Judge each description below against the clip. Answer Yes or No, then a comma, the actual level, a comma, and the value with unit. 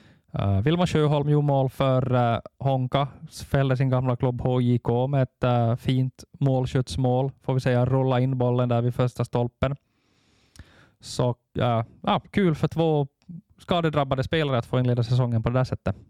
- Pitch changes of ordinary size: No, narrow, 2.1 semitones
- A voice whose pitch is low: Yes, low, 130 Hz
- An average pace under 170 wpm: Yes, average, 160 wpm